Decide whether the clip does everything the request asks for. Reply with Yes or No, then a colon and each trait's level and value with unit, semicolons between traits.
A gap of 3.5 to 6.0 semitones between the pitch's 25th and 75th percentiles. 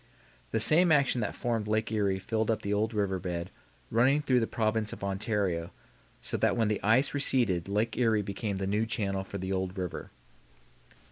No: average, 2.8 semitones